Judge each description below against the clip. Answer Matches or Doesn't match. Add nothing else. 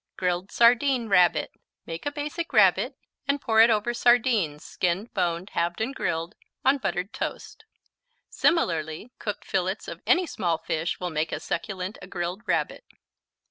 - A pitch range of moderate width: Doesn't match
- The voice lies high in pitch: Matches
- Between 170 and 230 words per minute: Doesn't match